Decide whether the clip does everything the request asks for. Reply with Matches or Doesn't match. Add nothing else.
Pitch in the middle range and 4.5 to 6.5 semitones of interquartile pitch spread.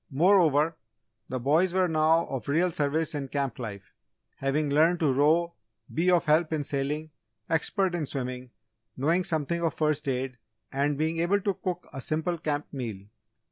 Doesn't match